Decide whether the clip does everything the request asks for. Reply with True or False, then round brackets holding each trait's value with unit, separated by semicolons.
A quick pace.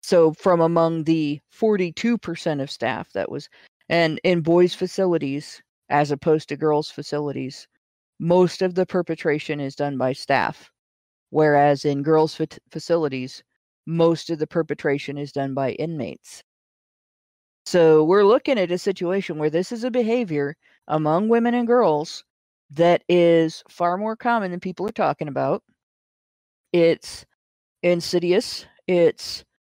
False (135 wpm)